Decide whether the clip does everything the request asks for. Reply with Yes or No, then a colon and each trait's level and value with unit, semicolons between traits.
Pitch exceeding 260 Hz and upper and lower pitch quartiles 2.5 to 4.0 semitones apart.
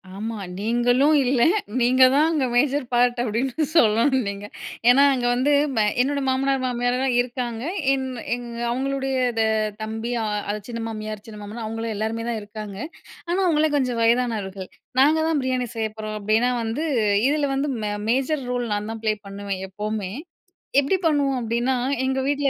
No: high, 245 Hz; average, 3.5 semitones